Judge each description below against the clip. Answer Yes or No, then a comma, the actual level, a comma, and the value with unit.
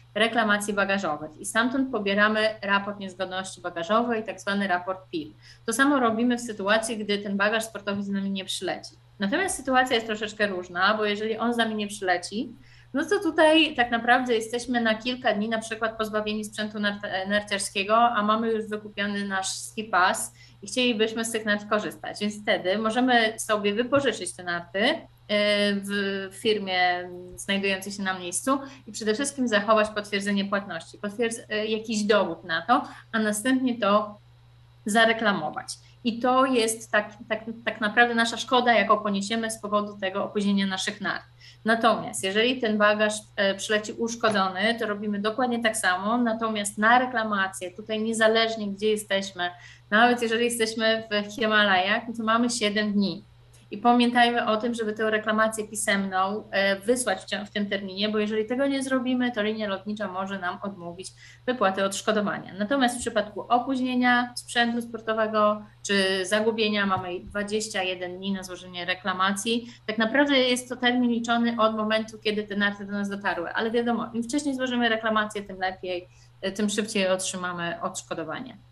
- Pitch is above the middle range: Yes, high, 215 Hz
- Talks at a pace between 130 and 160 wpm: Yes, average, 155 wpm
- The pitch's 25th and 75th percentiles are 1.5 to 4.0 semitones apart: Yes, narrow, 2.6 semitones